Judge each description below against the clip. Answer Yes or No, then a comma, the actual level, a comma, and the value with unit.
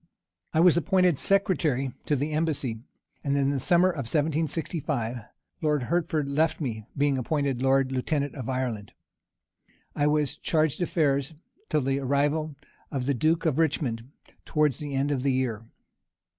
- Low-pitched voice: No, medium, 145 Hz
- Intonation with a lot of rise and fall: No, average, 3.2 semitones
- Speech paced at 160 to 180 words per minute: No, average, 145 wpm